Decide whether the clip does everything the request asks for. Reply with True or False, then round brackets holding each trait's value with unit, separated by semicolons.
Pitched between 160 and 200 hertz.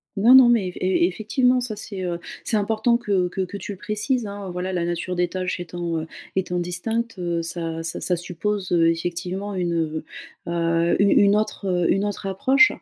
True (185 Hz)